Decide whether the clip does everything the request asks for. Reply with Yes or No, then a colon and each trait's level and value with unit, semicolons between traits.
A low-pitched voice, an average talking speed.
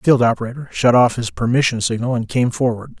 No: low, 120 Hz; fast, 220 wpm